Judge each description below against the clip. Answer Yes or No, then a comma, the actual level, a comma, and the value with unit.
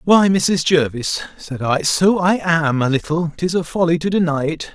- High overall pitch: No, medium, 165 Hz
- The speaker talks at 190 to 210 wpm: Yes, average, 200 wpm